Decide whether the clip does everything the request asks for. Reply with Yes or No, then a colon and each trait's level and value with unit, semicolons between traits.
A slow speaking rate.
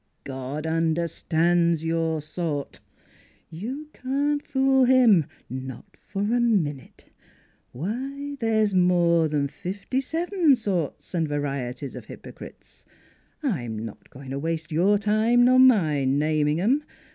Yes: slow, 120 wpm